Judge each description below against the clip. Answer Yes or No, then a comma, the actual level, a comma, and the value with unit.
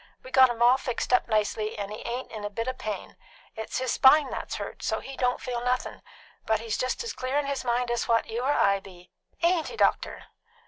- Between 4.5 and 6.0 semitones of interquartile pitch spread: No, average, 2.9 semitones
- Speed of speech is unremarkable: No, fast, 235 wpm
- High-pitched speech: Yes, high, 245 Hz